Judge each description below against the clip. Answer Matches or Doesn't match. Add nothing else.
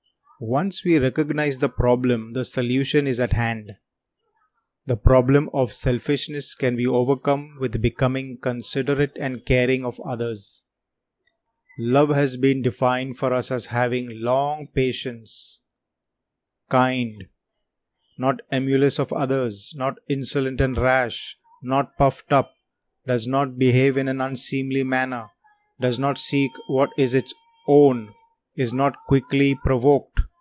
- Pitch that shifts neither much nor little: Doesn't match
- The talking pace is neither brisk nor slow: Matches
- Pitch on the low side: Matches